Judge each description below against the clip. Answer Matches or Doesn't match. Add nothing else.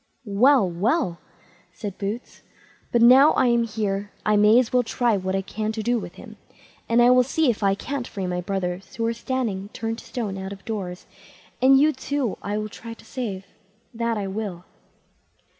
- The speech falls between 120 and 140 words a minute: Doesn't match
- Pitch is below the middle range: Doesn't match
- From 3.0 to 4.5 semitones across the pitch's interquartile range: Matches